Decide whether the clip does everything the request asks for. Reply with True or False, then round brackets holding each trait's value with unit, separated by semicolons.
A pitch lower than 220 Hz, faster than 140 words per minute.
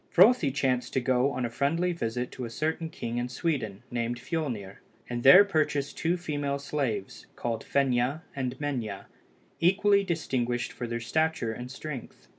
True (135 Hz; 160 wpm)